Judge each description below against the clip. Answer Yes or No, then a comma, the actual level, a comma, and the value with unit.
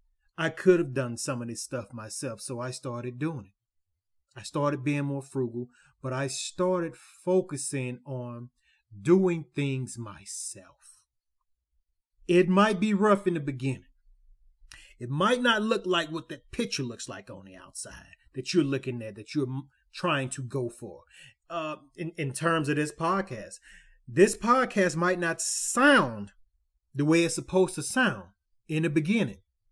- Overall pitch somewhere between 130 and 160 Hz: Yes, medium, 140 Hz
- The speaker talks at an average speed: Yes, average, 160 wpm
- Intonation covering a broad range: Yes, wide, 6.2 semitones